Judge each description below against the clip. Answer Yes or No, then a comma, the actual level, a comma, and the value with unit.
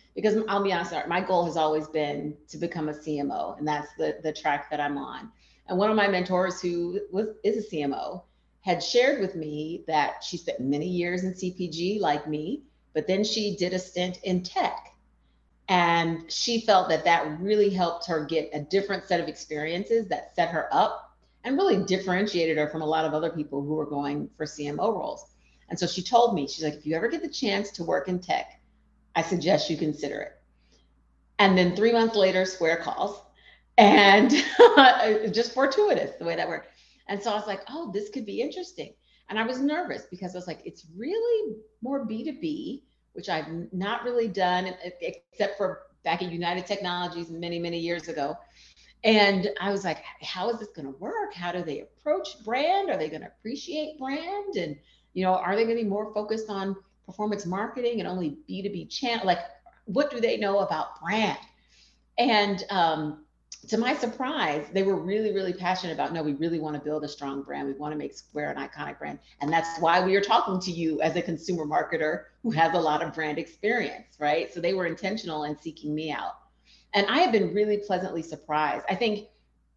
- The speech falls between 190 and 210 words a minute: Yes, average, 200 wpm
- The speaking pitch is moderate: Yes, medium, 180 Hz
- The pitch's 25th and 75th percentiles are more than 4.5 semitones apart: Yes, average, 5.2 semitones